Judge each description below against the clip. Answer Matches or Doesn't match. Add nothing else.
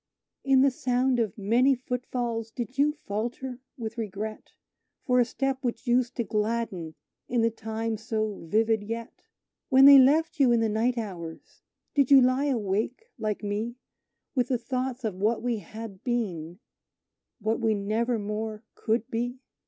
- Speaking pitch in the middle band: Doesn't match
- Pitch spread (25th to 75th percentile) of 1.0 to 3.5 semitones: Matches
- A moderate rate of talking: Matches